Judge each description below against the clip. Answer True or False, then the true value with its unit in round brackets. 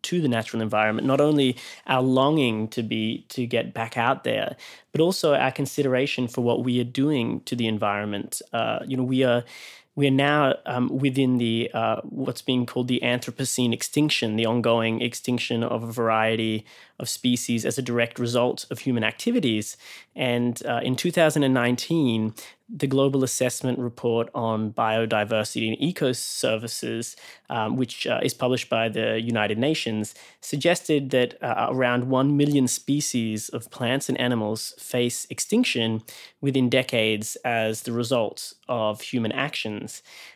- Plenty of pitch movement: False (2.7 semitones)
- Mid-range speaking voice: False (125 Hz)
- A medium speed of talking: True (155 wpm)